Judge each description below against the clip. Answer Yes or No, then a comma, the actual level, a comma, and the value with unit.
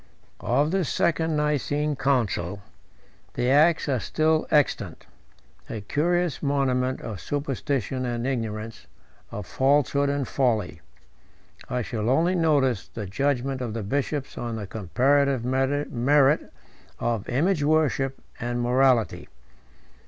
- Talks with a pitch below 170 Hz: Yes, low, 135 Hz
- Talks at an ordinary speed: No, slow, 115 wpm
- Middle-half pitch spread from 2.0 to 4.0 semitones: Yes, average, 3.5 semitones